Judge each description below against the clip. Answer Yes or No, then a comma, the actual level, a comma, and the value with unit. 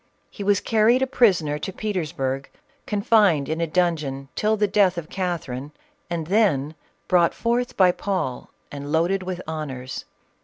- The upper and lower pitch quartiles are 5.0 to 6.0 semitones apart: Yes, average, 5.3 semitones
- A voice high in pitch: No, medium, 175 Hz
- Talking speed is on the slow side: No, average, 150 wpm